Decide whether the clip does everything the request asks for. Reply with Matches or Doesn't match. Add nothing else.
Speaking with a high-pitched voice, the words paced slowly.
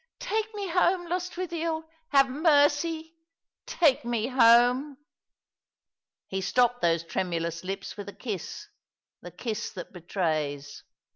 Matches